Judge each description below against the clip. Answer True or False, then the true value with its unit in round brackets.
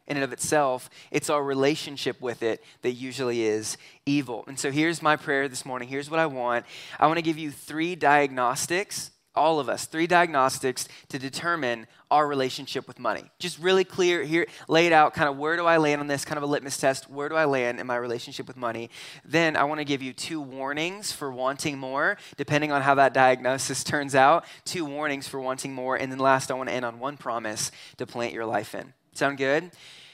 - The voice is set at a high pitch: False (140 Hz)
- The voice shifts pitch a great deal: False (2.9 semitones)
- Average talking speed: False (220 wpm)